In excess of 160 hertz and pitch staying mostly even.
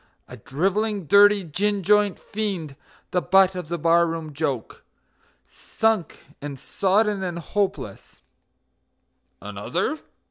No: medium, 185 Hz; average, 4.0 semitones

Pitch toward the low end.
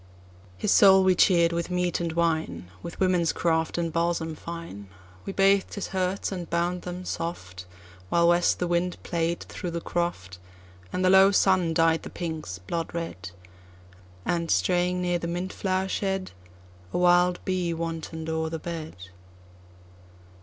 No: medium, 170 Hz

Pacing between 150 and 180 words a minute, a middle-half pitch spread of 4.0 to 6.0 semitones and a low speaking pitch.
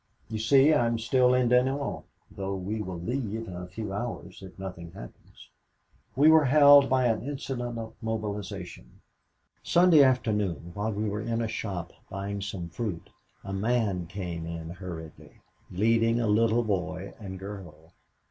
Yes: average, 155 wpm; average, 4.3 semitones; low, 105 Hz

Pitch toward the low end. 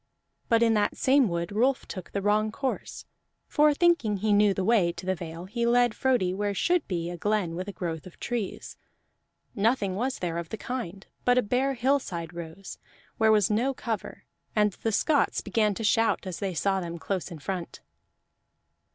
No: high, 205 Hz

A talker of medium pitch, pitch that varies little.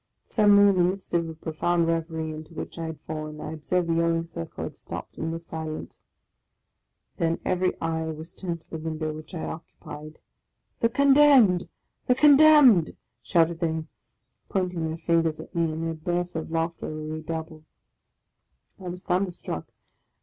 Yes: medium, 165 Hz; narrow, 2.2 semitones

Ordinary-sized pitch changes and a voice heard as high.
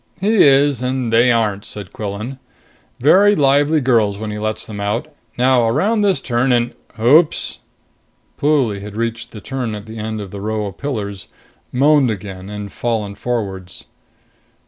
No: average, 4.5 semitones; low, 115 Hz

